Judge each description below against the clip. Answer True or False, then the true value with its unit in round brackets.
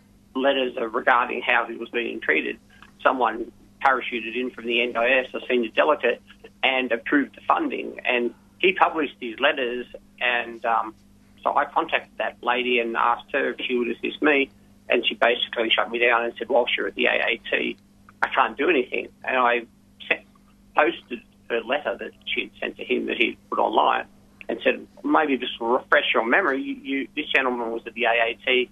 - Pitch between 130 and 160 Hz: False (120 Hz)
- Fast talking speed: False (185 wpm)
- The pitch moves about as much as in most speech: False (1.6 semitones)